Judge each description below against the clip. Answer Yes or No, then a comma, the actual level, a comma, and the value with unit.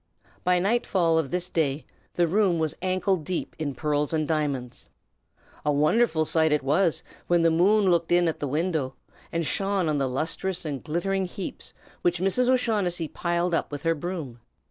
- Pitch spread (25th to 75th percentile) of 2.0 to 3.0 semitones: No, average, 3.5 semitones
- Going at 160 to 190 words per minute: Yes, average, 175 wpm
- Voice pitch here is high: No, medium, 170 Hz